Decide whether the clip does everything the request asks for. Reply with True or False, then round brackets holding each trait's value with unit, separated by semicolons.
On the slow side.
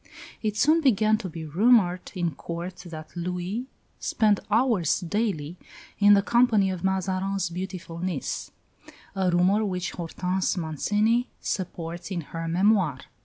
True (130 wpm)